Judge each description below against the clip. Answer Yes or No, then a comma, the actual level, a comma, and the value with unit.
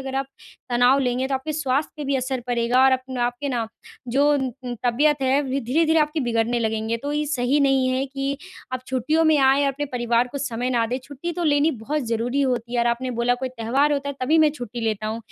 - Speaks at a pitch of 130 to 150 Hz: No, very high, 260 Hz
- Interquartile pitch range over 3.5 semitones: No, average, 2.9 semitones